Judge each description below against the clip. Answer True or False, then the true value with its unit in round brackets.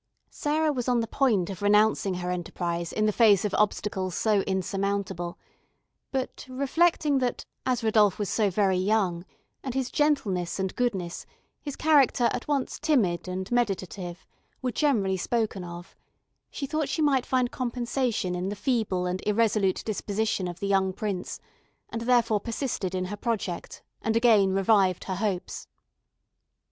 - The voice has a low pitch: False (210 Hz)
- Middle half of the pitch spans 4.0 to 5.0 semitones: True (4.7 semitones)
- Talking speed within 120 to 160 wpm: True (150 wpm)